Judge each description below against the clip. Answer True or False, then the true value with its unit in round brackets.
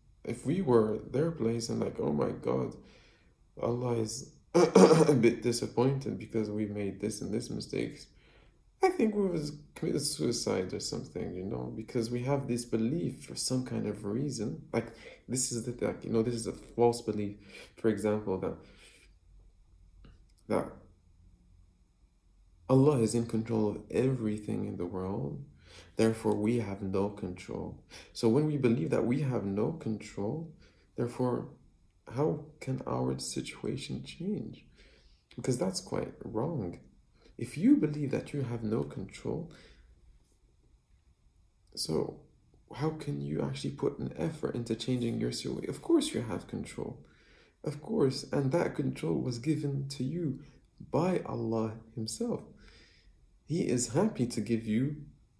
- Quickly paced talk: False (145 wpm)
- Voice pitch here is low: True (110 Hz)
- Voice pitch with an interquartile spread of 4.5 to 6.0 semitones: True (4.9 semitones)